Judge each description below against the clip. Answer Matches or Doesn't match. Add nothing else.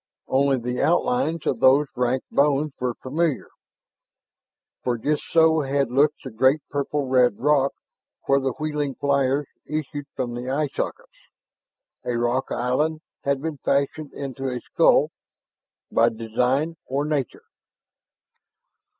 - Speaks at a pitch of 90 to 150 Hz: Matches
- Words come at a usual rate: Doesn't match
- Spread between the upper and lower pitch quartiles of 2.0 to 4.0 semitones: Matches